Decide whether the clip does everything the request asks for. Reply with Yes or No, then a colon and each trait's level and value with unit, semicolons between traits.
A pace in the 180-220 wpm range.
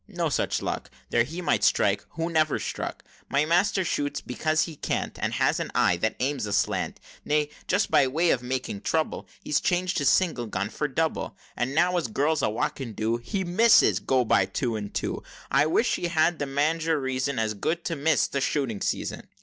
Yes: fast, 205 wpm